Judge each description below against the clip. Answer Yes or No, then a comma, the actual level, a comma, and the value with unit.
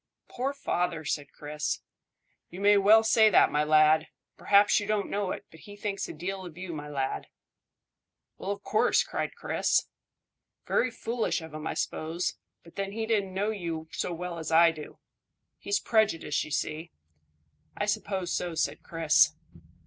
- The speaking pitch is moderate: Yes, medium, 180 Hz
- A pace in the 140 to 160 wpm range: No, average, 170 wpm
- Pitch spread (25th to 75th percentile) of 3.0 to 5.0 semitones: Yes, average, 4.5 semitones